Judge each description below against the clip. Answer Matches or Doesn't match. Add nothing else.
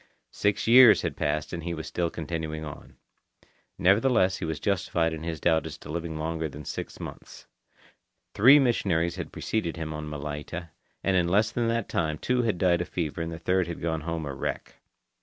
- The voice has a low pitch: Matches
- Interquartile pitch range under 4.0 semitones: Matches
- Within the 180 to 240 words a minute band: Matches